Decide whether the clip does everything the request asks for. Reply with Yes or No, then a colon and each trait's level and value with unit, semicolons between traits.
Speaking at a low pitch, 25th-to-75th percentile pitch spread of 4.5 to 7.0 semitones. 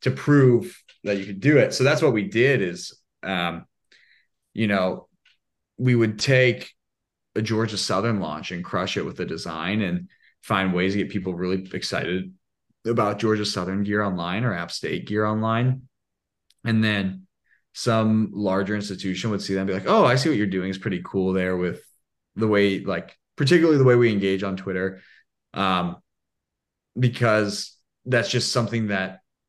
No: low, 100 Hz; average, 3.6 semitones